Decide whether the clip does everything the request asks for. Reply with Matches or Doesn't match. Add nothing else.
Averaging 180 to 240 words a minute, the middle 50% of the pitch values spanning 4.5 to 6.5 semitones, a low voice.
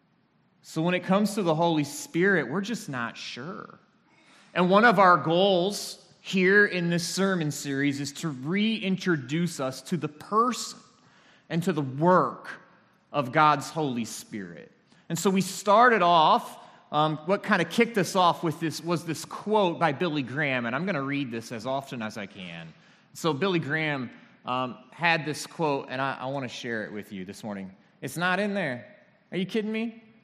Doesn't match